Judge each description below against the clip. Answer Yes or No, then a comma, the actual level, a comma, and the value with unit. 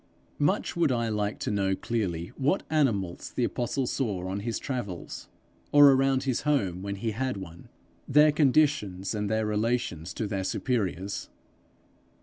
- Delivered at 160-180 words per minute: No, average, 150 wpm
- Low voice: Yes, low, 110 Hz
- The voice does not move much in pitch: No, wide, 5.4 semitones